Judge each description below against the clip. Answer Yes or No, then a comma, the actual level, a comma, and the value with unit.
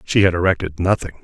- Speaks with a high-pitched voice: No, very low, 90 Hz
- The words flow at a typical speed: Yes, average, 195 wpm